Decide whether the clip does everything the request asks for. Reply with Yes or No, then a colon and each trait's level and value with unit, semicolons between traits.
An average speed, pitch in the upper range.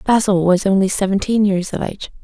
Yes: average, 190 wpm; high, 195 Hz